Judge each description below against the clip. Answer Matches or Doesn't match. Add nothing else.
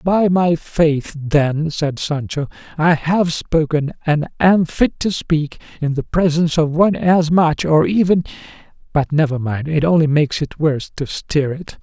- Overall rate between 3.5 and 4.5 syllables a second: Matches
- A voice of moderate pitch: Matches